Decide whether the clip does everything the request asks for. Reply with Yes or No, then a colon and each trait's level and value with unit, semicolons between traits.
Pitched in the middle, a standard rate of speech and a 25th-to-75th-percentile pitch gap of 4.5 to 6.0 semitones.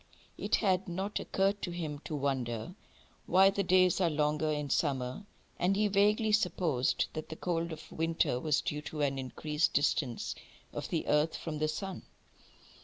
No: medium, 160 Hz; average, 170 wpm; average, 4.0 semitones